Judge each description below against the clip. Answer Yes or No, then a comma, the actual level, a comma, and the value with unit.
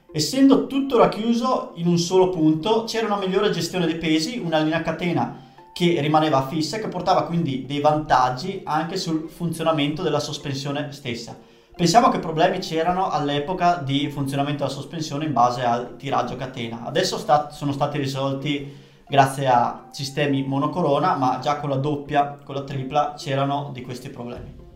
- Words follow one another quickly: No, average, 160 wpm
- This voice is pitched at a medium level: Yes, medium, 150 Hz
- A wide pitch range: No, average, 3.9 semitones